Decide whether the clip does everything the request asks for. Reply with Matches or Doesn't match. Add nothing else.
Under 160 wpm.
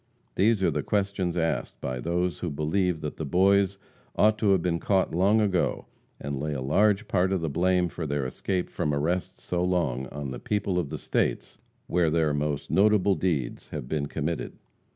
Doesn't match